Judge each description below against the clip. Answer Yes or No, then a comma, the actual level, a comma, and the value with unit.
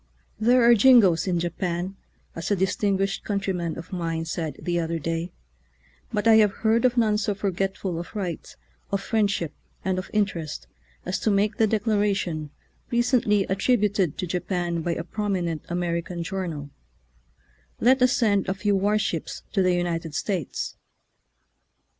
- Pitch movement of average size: Yes, average, 3.6 semitones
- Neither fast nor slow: Yes, average, 155 wpm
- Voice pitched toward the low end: No, high, 190 Hz